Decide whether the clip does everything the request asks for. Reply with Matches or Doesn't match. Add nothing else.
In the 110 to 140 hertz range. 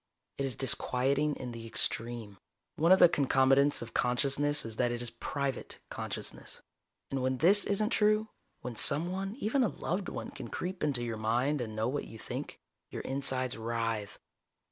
Matches